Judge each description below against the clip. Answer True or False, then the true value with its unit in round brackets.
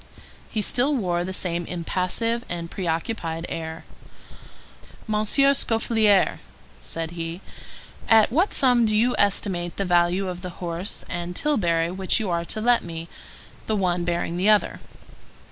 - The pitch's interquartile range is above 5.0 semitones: False (4.2 semitones)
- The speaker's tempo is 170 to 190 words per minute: False (145 wpm)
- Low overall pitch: False (185 Hz)